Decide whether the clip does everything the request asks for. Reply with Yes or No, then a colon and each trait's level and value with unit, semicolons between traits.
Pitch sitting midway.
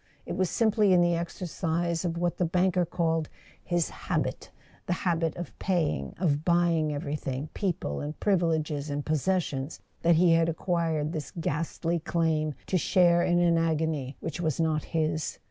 Yes: medium, 165 Hz